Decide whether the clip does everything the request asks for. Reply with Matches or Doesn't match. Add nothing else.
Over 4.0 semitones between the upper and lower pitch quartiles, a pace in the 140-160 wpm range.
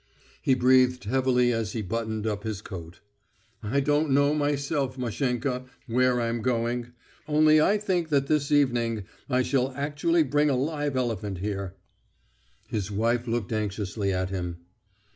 Matches